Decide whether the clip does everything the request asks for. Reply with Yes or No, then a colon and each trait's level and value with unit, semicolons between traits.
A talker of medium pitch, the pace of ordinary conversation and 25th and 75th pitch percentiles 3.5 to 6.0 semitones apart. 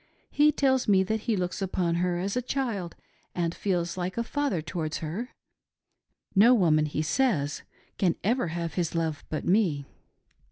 Yes: medium, 180 Hz; average, 165 wpm; average, 5.2 semitones